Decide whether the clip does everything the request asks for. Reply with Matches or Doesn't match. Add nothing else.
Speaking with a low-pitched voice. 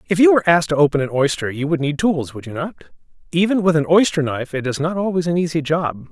Doesn't match